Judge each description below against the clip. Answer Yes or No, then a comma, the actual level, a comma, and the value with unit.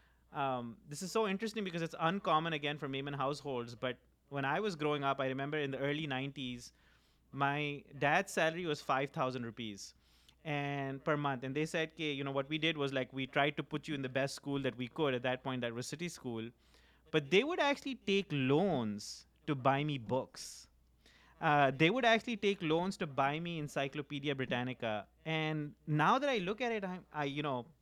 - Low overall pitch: No, medium, 145 Hz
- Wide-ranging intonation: No, average, 3.6 semitones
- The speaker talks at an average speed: No, fast, 195 wpm